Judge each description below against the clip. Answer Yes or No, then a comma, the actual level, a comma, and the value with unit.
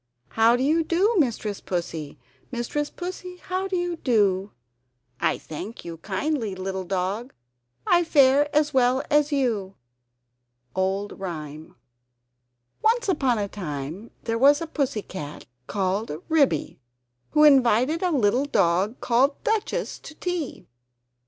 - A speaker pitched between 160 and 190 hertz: No, high, 245 Hz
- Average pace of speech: No, slow, 130 wpm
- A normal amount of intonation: No, wide, 7.8 semitones